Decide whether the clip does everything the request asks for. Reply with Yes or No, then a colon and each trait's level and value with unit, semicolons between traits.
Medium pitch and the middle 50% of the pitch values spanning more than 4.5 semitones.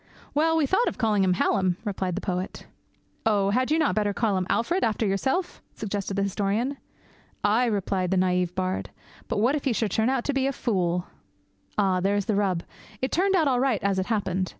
No: high, 205 Hz; average, 5.2 semitones